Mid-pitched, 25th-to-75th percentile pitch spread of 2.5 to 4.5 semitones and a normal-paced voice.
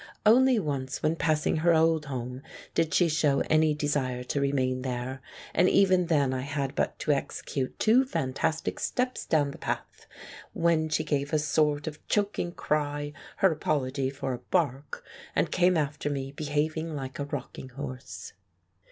Yes: medium, 150 Hz; average, 2.8 semitones; average, 160 wpm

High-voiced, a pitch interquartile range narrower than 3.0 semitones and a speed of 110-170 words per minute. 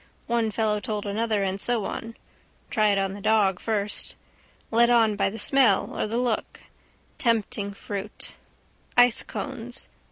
Yes: high, 220 Hz; narrow, 2.5 semitones; average, 150 wpm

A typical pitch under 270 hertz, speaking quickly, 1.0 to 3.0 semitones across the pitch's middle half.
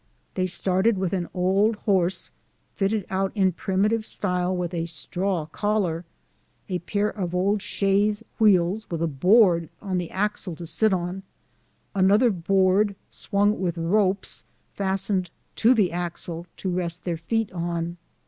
No: high, 190 Hz; average, 145 wpm; average, 2.7 semitones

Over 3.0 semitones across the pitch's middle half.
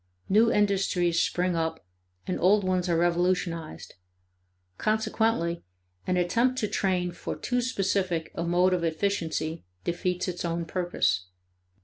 No: average, 2.7 semitones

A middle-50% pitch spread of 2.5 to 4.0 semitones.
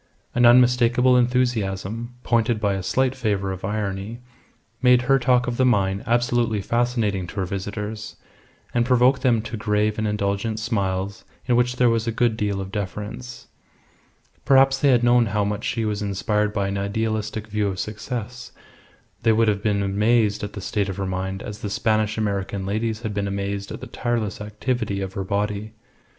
Yes: average, 3.1 semitones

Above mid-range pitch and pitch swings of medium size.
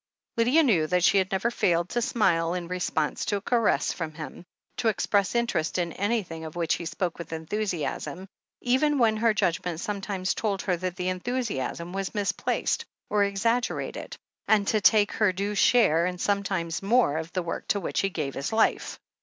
Yes: high, 195 Hz; average, 4.2 semitones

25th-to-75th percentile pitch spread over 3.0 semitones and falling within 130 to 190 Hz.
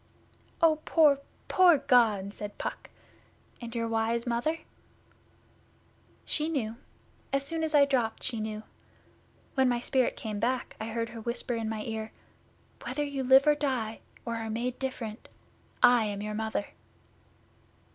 No: average, 3.7 semitones; high, 235 Hz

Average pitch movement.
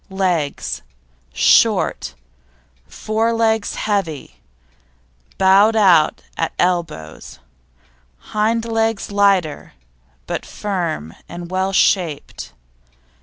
Yes: average, 4.4 semitones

